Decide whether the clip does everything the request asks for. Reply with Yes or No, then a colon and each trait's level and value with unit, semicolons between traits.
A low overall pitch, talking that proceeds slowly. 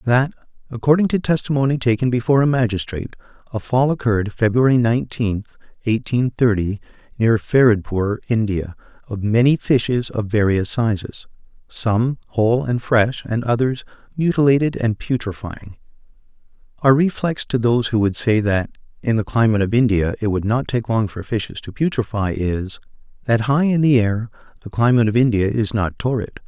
No: low, 115 Hz; average, 150 wpm